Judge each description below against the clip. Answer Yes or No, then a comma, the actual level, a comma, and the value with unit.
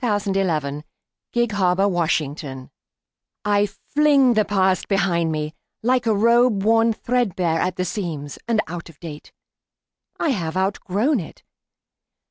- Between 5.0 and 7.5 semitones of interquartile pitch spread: Yes, average, 5.3 semitones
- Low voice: No, high, 195 Hz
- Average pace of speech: No, slow, 130 wpm